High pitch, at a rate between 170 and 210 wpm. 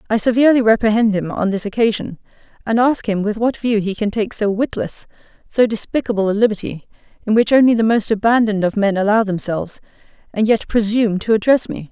Yes: high, 215 Hz; average, 190 wpm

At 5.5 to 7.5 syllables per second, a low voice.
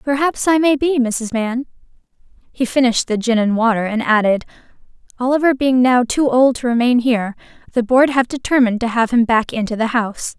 No: 5.6 syllables/s; high, 245 Hz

